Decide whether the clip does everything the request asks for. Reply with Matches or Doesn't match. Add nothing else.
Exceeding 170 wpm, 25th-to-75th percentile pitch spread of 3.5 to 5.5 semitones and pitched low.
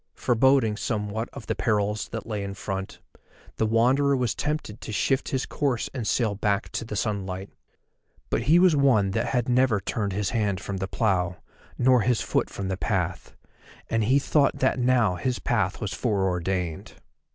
Matches